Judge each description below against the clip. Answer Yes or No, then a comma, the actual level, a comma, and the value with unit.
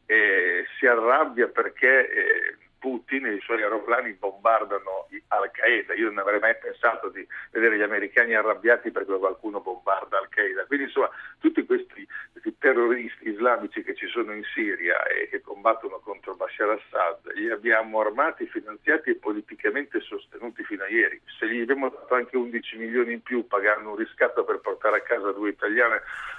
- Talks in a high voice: Yes, very high, 375 Hz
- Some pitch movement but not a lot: No, wide, 6.0 semitones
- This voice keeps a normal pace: No, fast, 175 wpm